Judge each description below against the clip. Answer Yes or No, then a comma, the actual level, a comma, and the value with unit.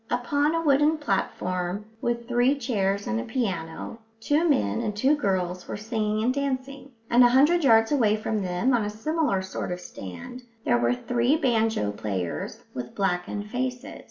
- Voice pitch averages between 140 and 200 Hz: No, high, 225 Hz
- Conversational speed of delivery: Yes, average, 170 wpm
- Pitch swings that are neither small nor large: No, wide, 6.0 semitones